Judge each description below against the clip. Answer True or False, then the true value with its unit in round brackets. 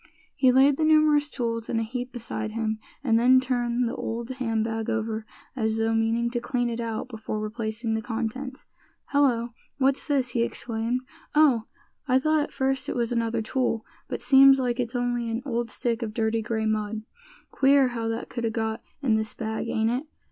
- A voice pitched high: True (235 Hz)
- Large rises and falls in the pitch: False (2.5 semitones)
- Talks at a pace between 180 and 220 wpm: True (195 wpm)